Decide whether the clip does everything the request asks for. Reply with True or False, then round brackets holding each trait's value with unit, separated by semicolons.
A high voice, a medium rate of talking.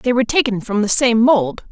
False (225 Hz; 245 wpm)